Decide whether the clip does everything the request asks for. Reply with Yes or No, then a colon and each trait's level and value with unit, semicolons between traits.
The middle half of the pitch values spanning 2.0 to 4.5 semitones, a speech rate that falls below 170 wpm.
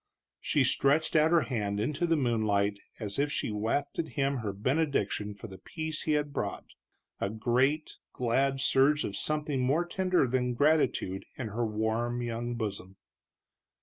No: average, 5.3 semitones; average, 155 wpm